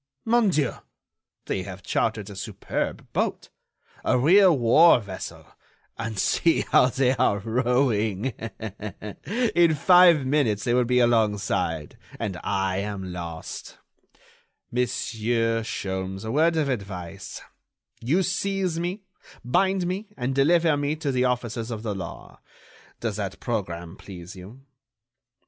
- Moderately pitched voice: No, low, 120 Hz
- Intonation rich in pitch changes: Yes, wide, 7.5 semitones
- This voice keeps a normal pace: No, slow, 130 wpm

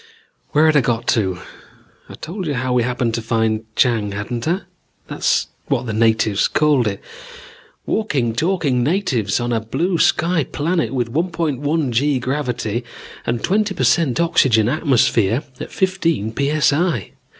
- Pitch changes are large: Yes, wide, 5.7 semitones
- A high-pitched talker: No, low, 130 Hz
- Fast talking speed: No, average, 150 wpm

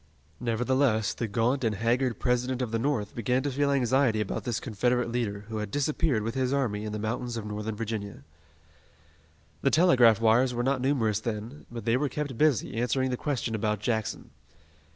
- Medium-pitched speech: No, low, 120 Hz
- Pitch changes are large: No, average, 3.1 semitones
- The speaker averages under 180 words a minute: No, average, 185 wpm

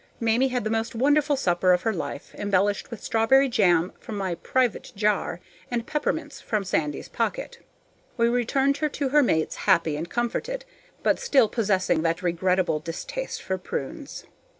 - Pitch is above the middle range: Yes, high, 220 Hz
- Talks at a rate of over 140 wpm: Yes, average, 160 wpm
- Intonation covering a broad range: Yes, wide, 6.6 semitones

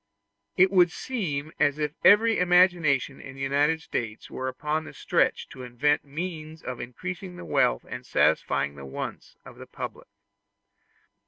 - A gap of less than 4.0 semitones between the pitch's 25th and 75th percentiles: No, average, 4.9 semitones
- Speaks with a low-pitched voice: No, medium, 150 Hz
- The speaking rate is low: No, average, 155 wpm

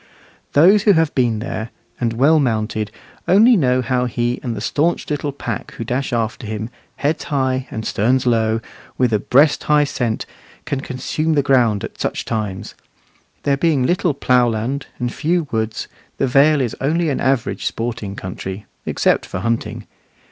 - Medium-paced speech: Yes, average, 165 wpm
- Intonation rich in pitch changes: No, average, 4.2 semitones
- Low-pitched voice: Yes, low, 125 Hz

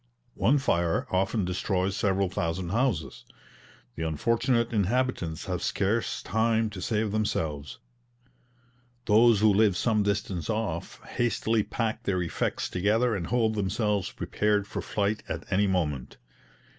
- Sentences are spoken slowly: Yes, slow, 130 wpm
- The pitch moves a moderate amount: Yes, average, 3.5 semitones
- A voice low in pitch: Yes, low, 105 Hz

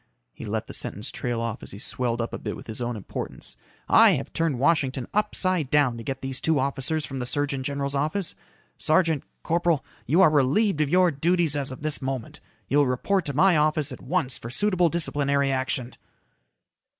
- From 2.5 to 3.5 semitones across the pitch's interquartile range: No, average, 4.1 semitones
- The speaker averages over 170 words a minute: Yes, average, 200 wpm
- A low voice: No, medium, 145 Hz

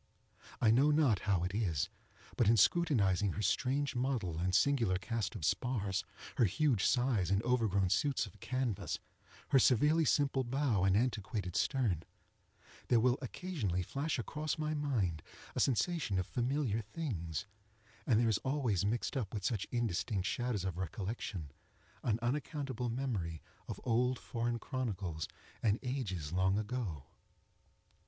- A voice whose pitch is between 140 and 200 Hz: No, low, 115 Hz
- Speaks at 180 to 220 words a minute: No, average, 145 wpm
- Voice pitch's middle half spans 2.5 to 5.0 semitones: No, wide, 5.5 semitones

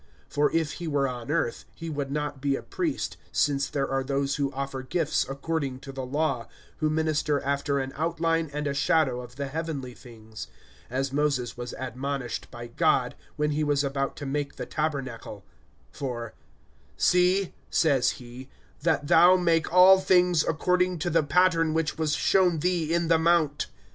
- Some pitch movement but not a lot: Yes, average, 3.3 semitones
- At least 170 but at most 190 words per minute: Yes, average, 175 wpm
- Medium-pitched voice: Yes, medium, 145 Hz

